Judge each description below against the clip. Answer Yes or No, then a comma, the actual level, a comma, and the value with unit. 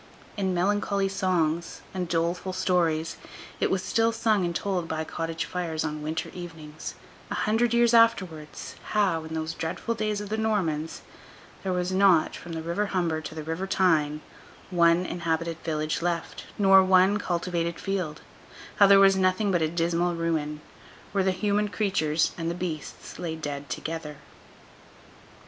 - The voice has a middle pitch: Yes, medium, 175 Hz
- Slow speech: No, average, 155 wpm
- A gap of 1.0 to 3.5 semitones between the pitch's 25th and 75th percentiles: Yes, average, 3.2 semitones